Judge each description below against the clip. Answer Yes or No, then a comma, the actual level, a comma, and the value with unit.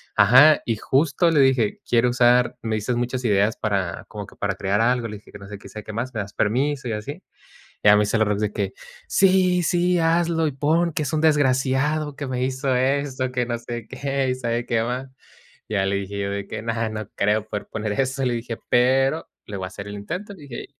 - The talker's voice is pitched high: No, low, 125 Hz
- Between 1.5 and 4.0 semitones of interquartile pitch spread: No, average, 4.6 semitones